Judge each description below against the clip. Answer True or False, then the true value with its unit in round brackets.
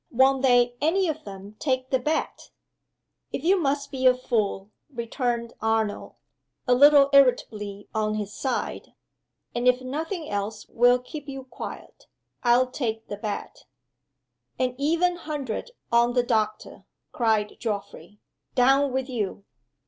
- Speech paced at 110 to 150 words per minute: True (135 wpm)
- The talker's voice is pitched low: False (250 Hz)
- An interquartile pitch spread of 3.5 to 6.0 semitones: True (3.9 semitones)